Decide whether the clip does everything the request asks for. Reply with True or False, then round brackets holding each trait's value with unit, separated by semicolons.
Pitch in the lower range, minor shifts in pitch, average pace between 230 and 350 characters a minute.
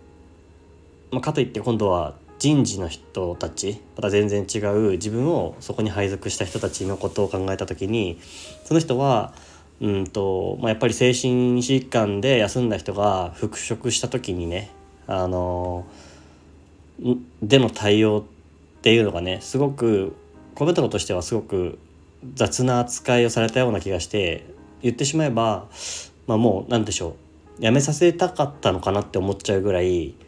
False (105 Hz; 5.1 semitones; 305 characters per minute)